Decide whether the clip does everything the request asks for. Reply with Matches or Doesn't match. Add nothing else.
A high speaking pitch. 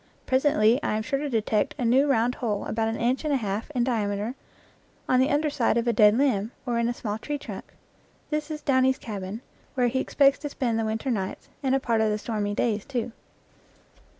Matches